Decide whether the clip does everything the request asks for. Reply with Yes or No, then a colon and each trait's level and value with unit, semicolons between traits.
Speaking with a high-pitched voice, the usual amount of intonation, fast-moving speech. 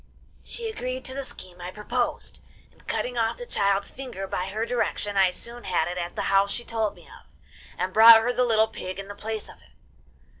Yes: high, 220 Hz; average, 3.9 semitones; fast, 220 wpm